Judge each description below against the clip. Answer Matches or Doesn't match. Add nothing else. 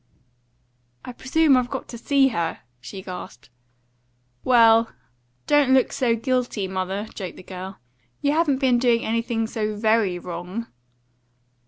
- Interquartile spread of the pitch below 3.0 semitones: Doesn't match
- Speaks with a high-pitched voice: Matches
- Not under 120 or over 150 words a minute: Matches